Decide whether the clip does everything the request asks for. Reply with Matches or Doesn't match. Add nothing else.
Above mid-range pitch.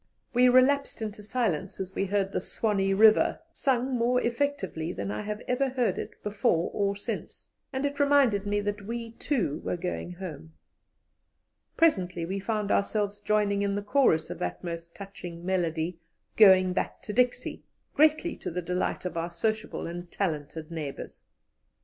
Matches